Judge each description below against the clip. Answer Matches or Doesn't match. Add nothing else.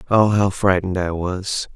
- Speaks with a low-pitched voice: Matches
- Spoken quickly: Doesn't match